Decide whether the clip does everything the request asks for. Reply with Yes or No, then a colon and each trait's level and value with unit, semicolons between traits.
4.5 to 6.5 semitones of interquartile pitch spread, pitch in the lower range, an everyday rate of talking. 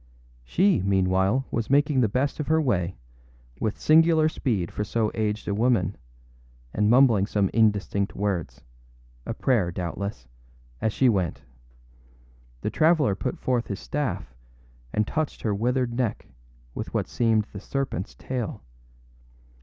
No: average, 5.1 semitones; low, 110 Hz; slow, 130 wpm